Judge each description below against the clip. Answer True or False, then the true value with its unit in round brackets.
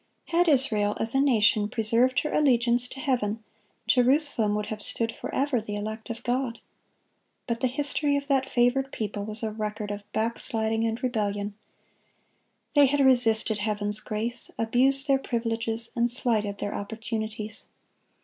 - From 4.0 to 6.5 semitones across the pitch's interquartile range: False (3.3 semitones)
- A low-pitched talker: False (230 Hz)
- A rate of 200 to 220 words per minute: False (150 wpm)